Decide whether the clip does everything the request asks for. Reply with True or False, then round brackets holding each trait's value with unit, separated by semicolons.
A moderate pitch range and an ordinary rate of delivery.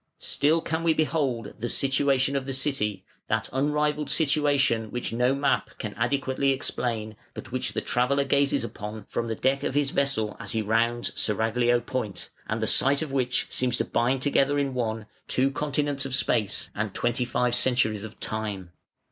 True (3.6 semitones; 175 wpm)